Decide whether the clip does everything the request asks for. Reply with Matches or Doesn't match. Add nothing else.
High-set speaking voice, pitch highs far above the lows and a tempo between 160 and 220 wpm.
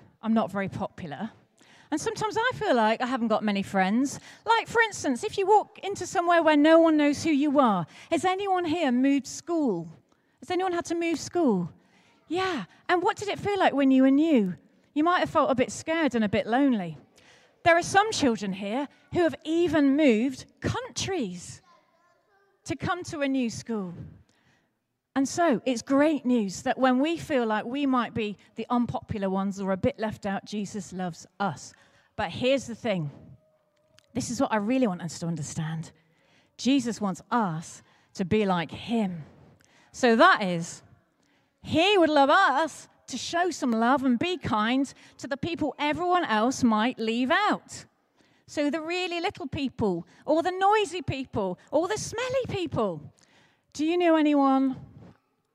Matches